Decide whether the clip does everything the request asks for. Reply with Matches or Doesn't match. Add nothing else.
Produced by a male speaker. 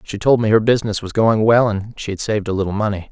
Matches